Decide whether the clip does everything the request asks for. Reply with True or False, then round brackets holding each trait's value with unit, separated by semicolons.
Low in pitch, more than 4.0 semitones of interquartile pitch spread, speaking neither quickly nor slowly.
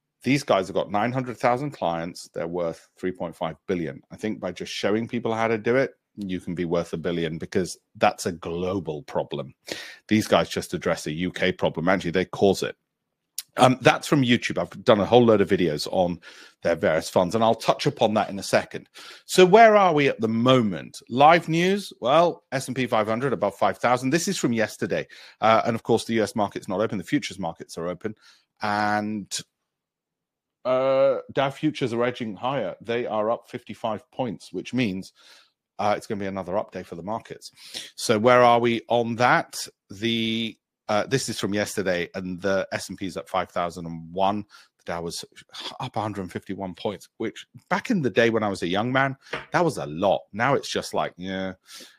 True (110 Hz; 4.5 semitones; 190 wpm)